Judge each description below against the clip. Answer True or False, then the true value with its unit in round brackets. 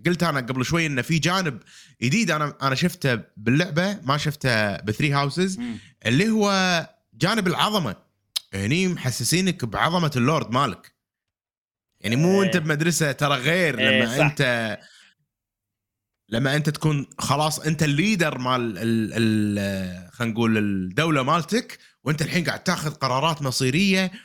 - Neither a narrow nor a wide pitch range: False (6.2 semitones)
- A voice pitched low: False (145 Hz)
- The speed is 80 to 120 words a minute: False (130 wpm)